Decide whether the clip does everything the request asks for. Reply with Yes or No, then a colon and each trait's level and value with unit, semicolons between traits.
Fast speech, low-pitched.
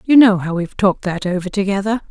No: fast, 230 wpm; high, 200 Hz